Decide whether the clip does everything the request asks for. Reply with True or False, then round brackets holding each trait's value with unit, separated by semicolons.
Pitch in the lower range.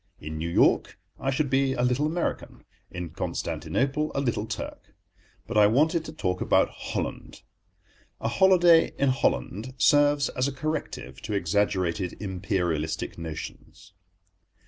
True (120 Hz)